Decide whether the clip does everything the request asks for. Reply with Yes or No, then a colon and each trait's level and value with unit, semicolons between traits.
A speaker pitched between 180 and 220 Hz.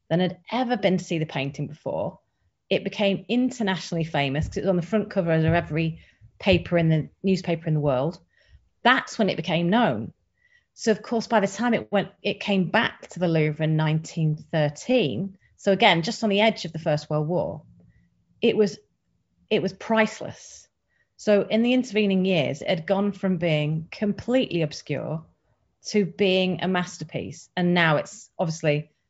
Yes: medium, 185 Hz